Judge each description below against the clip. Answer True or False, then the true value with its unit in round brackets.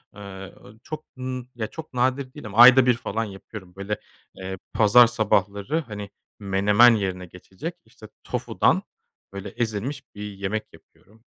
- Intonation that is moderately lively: True (3.9 semitones)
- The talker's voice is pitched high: False (105 Hz)